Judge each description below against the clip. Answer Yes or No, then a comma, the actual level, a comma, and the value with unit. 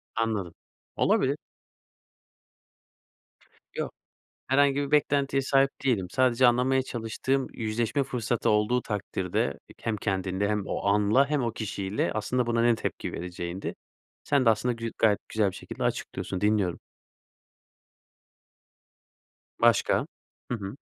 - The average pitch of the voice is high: No, low, 115 Hz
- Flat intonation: No, average, 4.1 semitones